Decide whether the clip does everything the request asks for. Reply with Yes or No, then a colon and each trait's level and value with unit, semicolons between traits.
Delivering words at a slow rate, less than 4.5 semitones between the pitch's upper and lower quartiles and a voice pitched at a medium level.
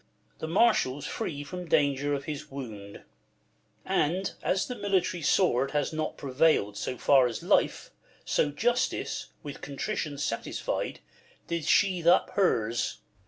No: slow, 130 wpm; average, 4.8 semitones; medium, 150 Hz